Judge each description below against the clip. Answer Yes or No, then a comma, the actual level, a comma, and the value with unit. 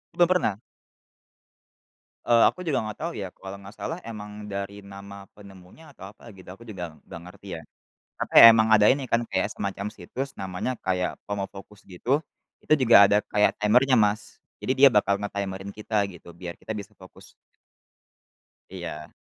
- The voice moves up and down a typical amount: No, narrow, 2.3 semitones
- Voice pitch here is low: Yes, low, 100 Hz